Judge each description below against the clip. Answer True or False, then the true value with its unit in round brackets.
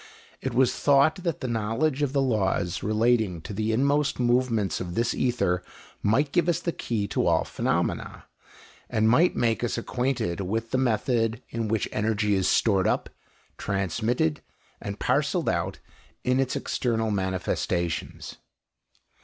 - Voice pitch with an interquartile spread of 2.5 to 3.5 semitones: False (4.0 semitones)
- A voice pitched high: False (115 Hz)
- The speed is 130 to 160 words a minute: True (145 wpm)